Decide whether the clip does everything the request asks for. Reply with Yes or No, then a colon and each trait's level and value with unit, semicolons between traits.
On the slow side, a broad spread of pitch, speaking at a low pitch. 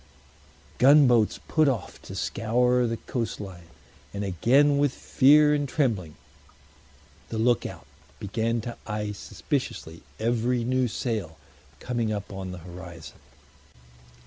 No: slow, 120 wpm; average, 4.2 semitones; low, 115 Hz